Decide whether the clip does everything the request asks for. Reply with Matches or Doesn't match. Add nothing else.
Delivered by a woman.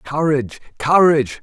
Doesn't match